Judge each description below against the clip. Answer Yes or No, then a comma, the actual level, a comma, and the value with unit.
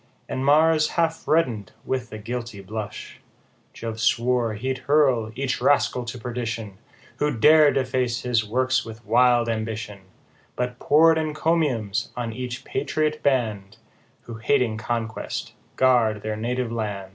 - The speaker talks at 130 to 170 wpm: Yes, slow, 135 wpm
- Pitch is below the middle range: Yes, low, 120 Hz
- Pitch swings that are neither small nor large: Yes, average, 3.1 semitones